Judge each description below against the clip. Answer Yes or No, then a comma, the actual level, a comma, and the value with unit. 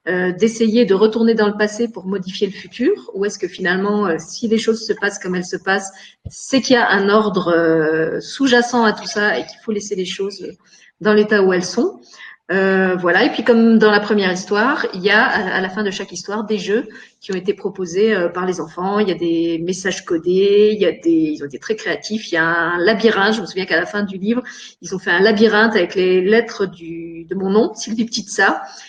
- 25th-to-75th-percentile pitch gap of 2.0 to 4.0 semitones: Yes, average, 3.1 semitones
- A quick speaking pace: Yes, fast, 235 wpm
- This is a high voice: Yes, high, 200 Hz